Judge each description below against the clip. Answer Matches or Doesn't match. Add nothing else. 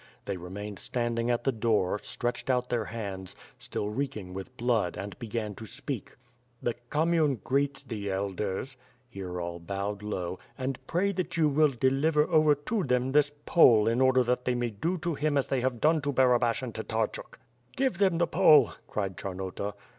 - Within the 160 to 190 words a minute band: Matches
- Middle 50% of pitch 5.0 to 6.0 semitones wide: Matches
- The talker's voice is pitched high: Doesn't match